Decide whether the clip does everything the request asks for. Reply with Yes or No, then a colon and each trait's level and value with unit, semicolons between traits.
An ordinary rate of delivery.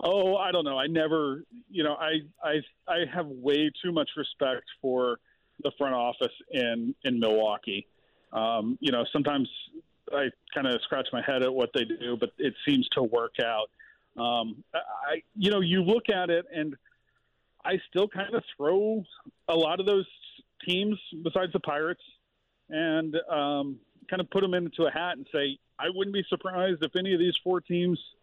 Yes: average, 185 wpm